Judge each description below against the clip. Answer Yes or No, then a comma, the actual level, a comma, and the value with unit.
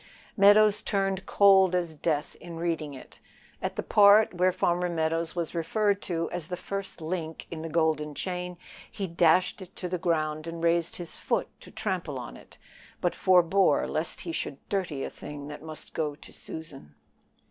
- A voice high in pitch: No, medium, 170 Hz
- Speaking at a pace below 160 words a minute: No, average, 180 wpm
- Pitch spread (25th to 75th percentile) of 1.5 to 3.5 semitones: Yes, average, 2.7 semitones